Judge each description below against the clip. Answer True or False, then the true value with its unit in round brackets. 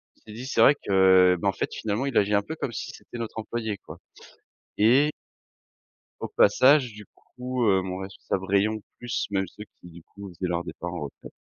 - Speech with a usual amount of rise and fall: True (3.9 semitones)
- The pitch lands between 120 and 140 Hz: False (105 Hz)